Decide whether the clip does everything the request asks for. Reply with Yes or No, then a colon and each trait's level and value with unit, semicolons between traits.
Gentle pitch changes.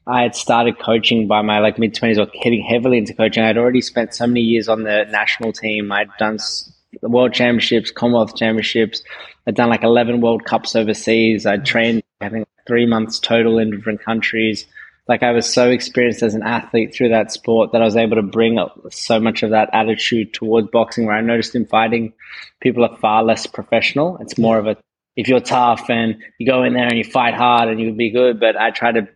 Yes: narrow, 1.3 semitones